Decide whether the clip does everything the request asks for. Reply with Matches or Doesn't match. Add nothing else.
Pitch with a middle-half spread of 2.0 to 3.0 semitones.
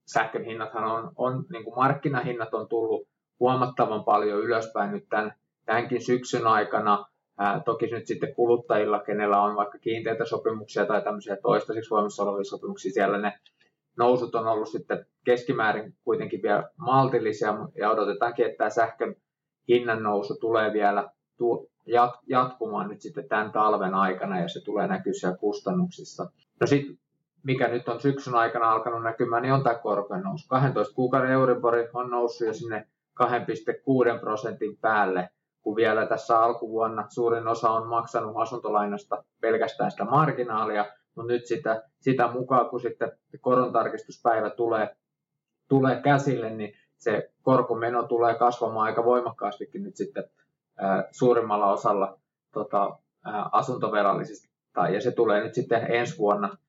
Matches